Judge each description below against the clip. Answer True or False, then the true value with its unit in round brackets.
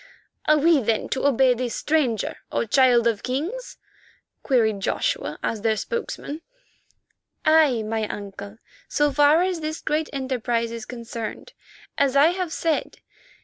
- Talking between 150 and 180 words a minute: False (140 wpm)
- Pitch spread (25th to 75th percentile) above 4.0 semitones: True (5.2 semitones)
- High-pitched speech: True (265 Hz)